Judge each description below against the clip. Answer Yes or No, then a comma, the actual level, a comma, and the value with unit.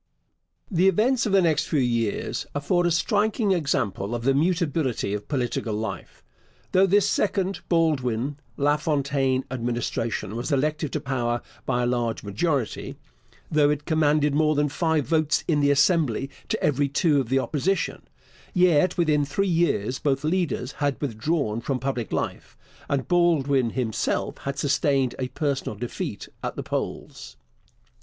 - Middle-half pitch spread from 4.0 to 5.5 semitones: Yes, average, 4.6 semitones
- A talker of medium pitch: Yes, medium, 145 Hz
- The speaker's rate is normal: Yes, average, 150 wpm